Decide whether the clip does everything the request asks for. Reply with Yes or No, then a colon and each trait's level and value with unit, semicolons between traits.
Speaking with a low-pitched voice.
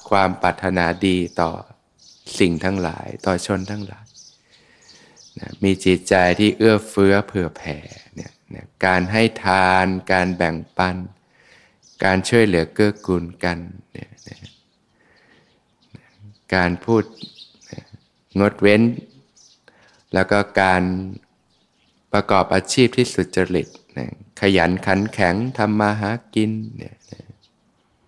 Yes: very low, 95 Hz